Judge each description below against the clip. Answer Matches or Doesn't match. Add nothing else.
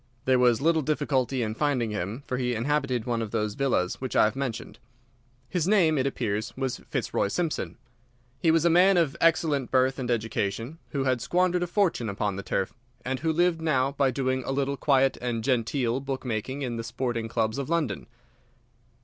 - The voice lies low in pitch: Matches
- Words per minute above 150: Matches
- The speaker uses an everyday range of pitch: Matches